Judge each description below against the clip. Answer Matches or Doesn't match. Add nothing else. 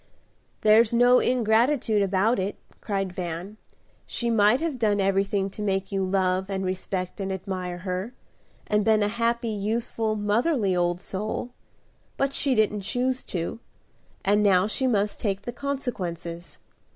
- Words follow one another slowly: Doesn't match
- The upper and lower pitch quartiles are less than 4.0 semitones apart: Matches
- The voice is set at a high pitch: Matches